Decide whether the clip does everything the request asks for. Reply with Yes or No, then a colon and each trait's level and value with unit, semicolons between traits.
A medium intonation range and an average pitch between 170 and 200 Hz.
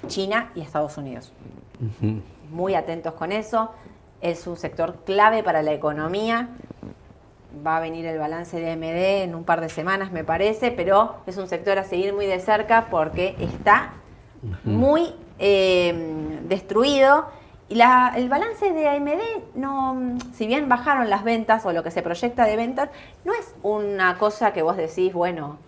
No: wide, 6.1 semitones; high, 190 Hz